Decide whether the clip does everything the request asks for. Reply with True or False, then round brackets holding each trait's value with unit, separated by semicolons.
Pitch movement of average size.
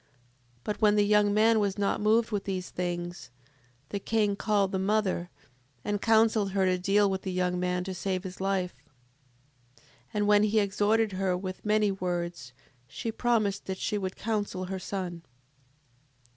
False (2.3 semitones)